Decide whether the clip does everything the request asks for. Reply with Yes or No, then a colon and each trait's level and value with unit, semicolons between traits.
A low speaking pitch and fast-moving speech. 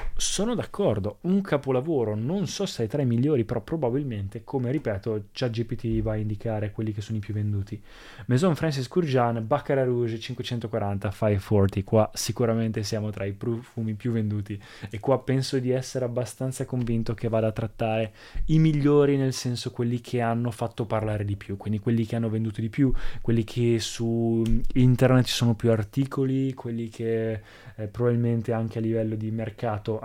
Yes: low, 115 Hz; fast, 175 wpm